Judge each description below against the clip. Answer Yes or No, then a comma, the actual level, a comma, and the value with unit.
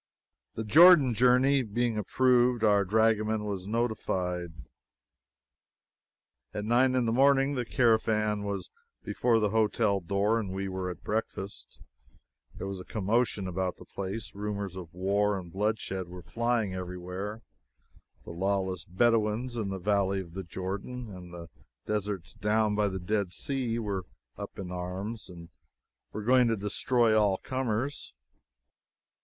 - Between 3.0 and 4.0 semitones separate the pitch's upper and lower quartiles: Yes, average, 3.4 semitones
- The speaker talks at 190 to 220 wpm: No, average, 145 wpm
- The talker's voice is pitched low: Yes, low, 105 Hz